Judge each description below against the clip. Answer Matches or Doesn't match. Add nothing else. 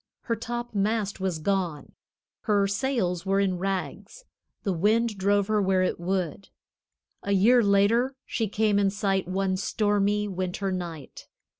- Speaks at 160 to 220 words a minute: Doesn't match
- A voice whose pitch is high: Matches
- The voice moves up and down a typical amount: Doesn't match